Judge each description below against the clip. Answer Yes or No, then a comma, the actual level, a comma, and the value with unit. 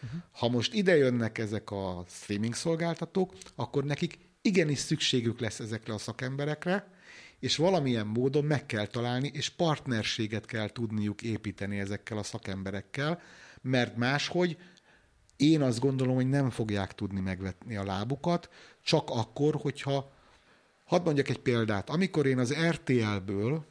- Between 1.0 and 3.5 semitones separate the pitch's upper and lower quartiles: No, wide, 5.6 semitones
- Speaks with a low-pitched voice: Yes, low, 130 Hz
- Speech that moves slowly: No, average, 135 wpm